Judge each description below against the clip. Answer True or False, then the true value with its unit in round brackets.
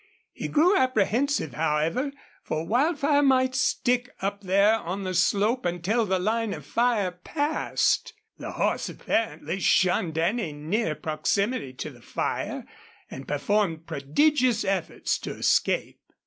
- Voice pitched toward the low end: False (200 Hz)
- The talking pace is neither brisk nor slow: False (130 wpm)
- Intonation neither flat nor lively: False (6.9 semitones)